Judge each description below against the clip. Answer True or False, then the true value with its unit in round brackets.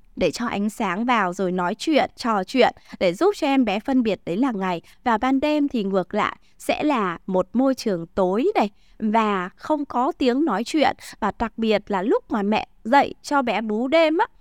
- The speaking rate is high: False (215 wpm)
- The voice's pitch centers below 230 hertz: False (235 Hz)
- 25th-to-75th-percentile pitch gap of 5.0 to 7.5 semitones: True (5.6 semitones)